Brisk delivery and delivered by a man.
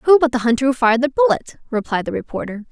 No: fast, 245 wpm; female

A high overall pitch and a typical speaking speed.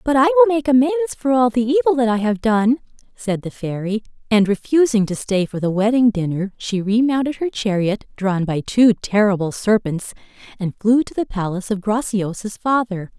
Yes: high, 230 Hz; average, 185 wpm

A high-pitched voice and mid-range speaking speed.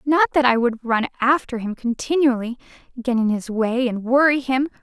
Yes: very high, 250 Hz; average, 185 wpm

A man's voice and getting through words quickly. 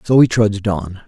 Yes: male; fast, 225 wpm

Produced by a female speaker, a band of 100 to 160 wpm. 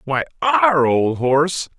No: male; slow, 135 wpm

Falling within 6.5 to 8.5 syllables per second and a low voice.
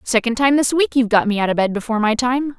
No: 6.8 syllables/s; high, 240 Hz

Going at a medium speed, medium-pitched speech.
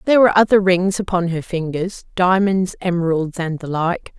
Yes: average, 160 wpm; medium, 180 Hz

